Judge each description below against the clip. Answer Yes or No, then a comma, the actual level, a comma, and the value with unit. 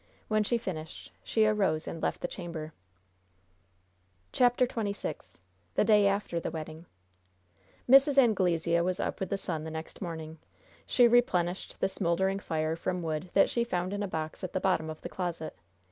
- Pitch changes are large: No, average, 4.2 semitones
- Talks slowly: No, average, 170 wpm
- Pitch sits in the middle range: Yes, medium, 180 Hz